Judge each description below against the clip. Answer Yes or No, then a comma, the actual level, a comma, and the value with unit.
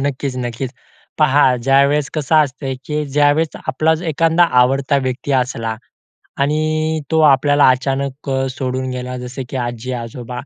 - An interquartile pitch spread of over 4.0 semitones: No, average, 2.8 semitones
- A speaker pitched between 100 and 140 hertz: Yes, low, 135 Hz